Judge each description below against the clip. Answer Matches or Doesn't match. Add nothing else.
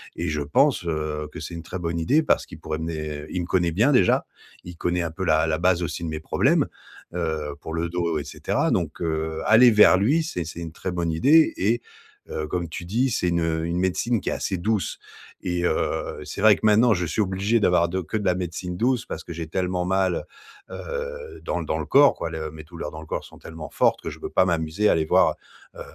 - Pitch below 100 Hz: Matches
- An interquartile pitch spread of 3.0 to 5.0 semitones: Matches